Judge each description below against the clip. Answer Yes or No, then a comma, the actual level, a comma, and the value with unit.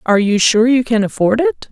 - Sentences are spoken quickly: Yes, fast, 245 wpm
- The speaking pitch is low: No, high, 235 Hz